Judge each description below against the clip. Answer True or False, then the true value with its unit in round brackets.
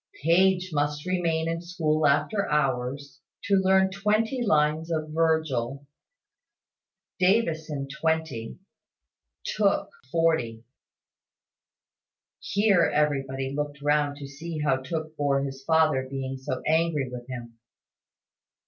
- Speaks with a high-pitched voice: False (150 Hz)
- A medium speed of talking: False (105 wpm)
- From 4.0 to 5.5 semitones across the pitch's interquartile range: False (3.5 semitones)